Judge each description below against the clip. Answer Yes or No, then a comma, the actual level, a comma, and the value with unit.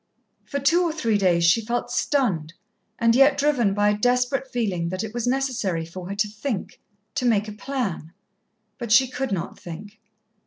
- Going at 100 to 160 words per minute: No, average, 185 wpm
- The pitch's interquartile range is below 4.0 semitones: No, average, 4.9 semitones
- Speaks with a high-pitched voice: Yes, high, 230 Hz